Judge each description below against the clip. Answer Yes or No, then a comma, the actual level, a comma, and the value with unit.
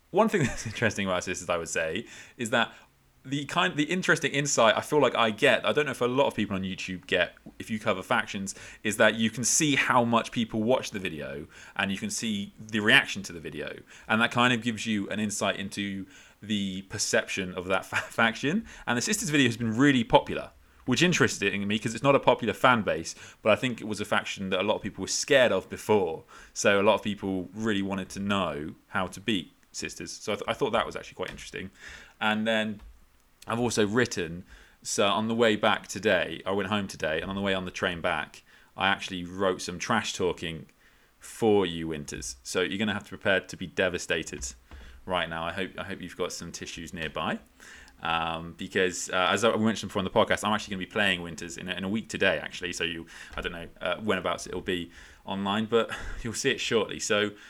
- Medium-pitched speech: No, low, 105 Hz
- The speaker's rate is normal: No, fast, 235 wpm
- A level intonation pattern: No, average, 3.7 semitones